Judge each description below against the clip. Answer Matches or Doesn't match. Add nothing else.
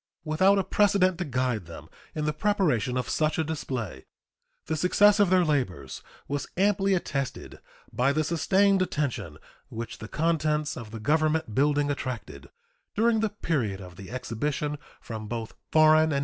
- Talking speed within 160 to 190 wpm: Matches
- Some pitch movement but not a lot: Doesn't match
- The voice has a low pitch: Doesn't match